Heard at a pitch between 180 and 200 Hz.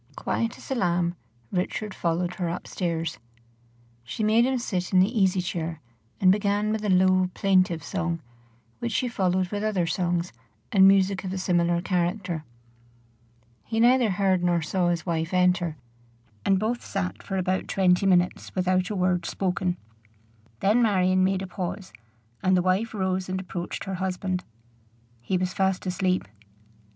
Yes: medium, 185 Hz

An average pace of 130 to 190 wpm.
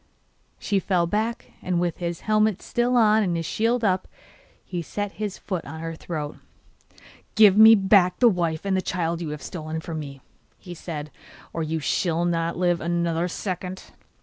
Yes: average, 175 wpm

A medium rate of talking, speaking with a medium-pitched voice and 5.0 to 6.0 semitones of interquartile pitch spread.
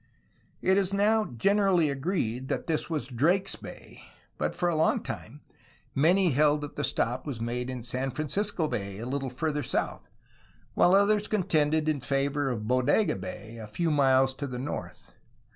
Yes: average, 170 wpm; medium, 145 Hz; wide, 5.5 semitones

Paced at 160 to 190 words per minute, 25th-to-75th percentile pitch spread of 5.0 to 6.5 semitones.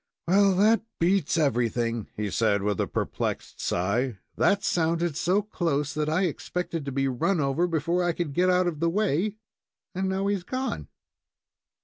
Yes: average, 165 wpm; wide, 5.5 semitones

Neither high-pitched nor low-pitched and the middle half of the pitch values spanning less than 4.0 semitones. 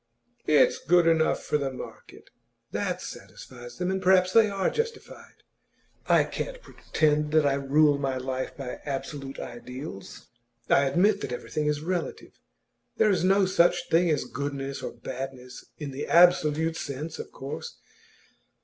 No: medium, 150 Hz; average, 4.6 semitones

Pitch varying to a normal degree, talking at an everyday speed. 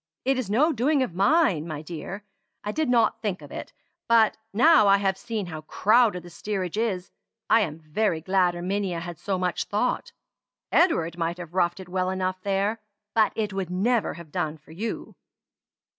Yes: average, 4.2 semitones; average, 185 wpm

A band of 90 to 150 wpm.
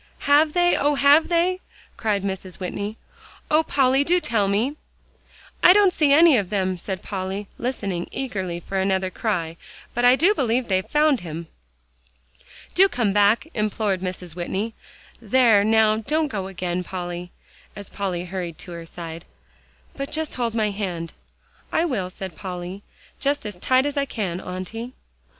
No: average, 160 wpm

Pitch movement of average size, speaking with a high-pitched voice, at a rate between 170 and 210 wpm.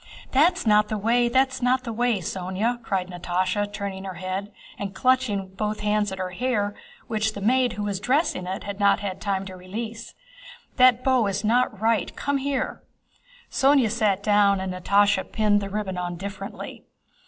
Yes: average, 3.8 semitones; high, 210 Hz; average, 175 wpm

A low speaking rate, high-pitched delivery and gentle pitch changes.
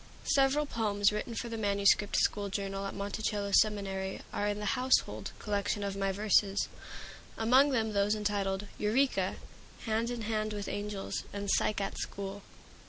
No: average, 155 wpm; high, 205 Hz; narrow, 1.7 semitones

